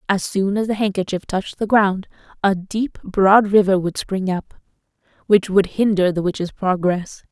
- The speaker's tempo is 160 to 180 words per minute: Yes, average, 170 wpm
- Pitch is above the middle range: Yes, high, 195 Hz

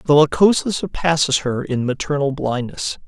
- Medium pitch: Yes, medium, 145 Hz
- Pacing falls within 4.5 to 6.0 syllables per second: Yes, 4.7 syllables/s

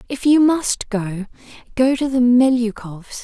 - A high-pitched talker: Yes, high, 245 Hz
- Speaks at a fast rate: No, average, 150 wpm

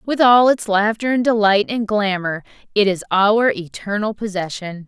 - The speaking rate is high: No, average, 160 wpm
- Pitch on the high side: Yes, high, 210 Hz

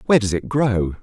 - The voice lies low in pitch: Yes, low, 110 Hz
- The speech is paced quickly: Yes, fast, 235 wpm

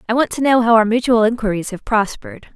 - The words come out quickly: Yes, fast, 235 wpm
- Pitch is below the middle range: No, high, 230 Hz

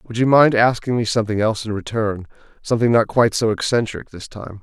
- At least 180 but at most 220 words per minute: Yes, average, 195 wpm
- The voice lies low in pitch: Yes, low, 110 Hz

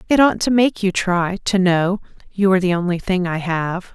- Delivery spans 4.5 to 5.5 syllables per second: Yes, 5.0 syllables/s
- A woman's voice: Yes, female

